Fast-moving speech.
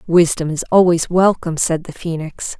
No: average, 160 wpm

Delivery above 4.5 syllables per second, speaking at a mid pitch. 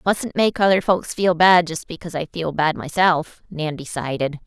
Yes: 4.8 syllables/s; medium, 170 Hz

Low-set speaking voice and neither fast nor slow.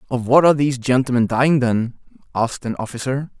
Yes: low, 130 Hz; average, 175 wpm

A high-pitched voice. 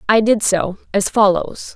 Yes: high, 205 Hz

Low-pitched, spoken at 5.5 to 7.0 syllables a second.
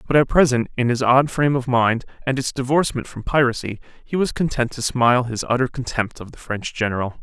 Yes: low, 125 Hz; 6.0 syllables/s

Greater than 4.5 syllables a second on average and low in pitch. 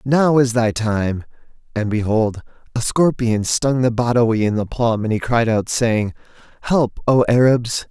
No: 4.2 syllables/s; low, 115 Hz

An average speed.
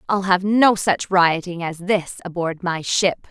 Yes: average, 180 wpm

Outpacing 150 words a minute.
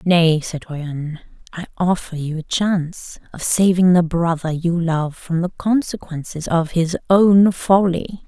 No: average, 145 wpm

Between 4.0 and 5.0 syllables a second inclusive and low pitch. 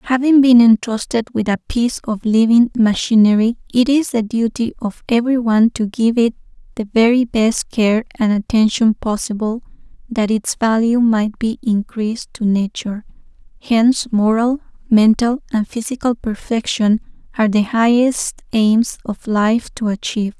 No: 4.6 syllables/s; high, 225 Hz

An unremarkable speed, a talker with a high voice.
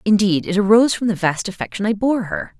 No: fast, 230 wpm; high, 195 Hz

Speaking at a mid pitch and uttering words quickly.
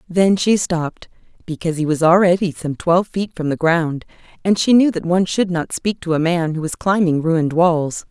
Yes: medium, 170 Hz; fast, 215 wpm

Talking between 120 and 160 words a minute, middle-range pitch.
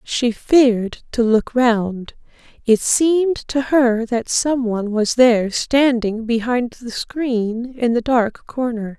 No: average, 140 wpm; high, 240 Hz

